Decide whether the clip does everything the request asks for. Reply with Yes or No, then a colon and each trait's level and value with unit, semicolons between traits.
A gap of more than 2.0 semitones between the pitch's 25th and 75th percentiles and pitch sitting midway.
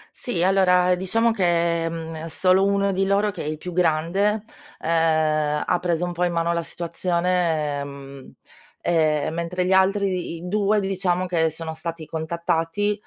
Yes: narrow, 2.6 semitones; medium, 175 Hz